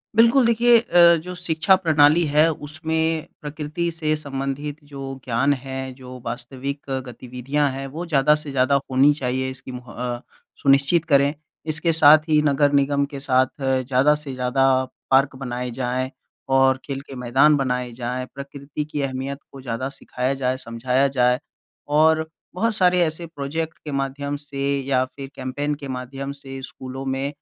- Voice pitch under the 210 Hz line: Yes, medium, 140 Hz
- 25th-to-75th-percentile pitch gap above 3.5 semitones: No, average, 2.7 semitones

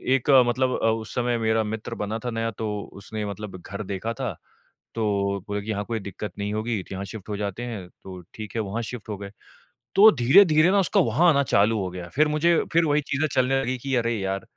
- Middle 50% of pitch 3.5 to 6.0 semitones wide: Yes, average, 4.0 semitones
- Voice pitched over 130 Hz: No, low, 110 Hz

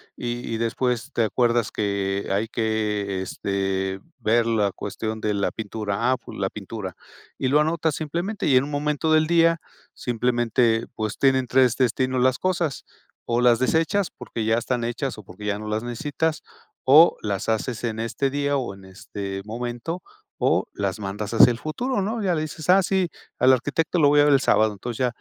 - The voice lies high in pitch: No, low, 120 Hz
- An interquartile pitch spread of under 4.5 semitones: No, average, 5.1 semitones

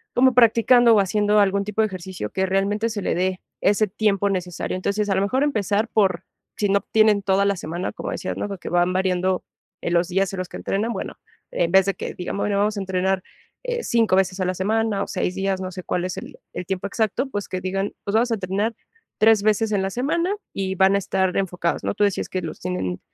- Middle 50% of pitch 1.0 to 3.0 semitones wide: Yes, narrow, 2.4 semitones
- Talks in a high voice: Yes, high, 195 Hz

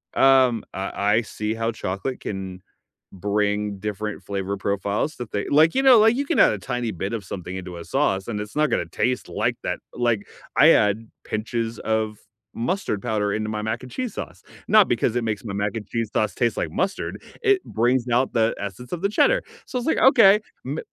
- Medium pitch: No, low, 110 Hz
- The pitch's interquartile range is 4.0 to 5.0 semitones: Yes, average, 4.3 semitones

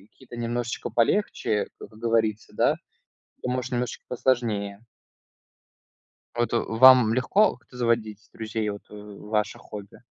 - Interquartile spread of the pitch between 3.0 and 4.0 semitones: No, narrow, 2.5 semitones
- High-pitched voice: No, low, 115 Hz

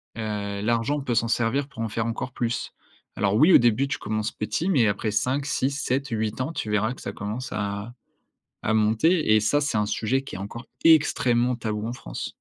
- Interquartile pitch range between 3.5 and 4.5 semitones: Yes, average, 3.8 semitones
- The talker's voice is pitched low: Yes, low, 115 Hz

